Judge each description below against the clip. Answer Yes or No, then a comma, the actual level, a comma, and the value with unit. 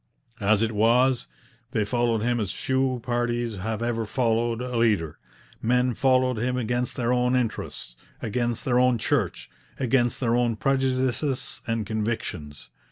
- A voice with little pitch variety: Yes, narrow, 2.2 semitones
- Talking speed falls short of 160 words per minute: Yes, average, 145 wpm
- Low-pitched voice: Yes, low, 120 Hz